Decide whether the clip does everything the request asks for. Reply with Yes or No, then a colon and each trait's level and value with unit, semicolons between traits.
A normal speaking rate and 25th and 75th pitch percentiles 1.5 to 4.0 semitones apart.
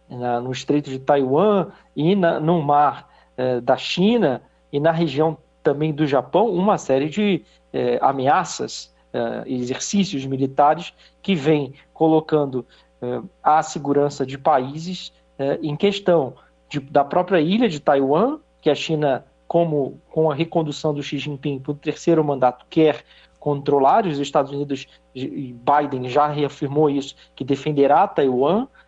Yes: average, 145 wpm; average, 3.1 semitones